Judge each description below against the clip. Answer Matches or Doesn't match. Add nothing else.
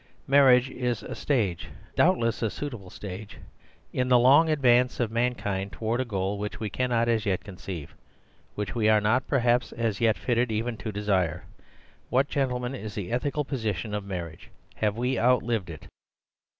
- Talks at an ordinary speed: Matches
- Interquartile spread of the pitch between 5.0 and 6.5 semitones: Doesn't match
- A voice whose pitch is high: Doesn't match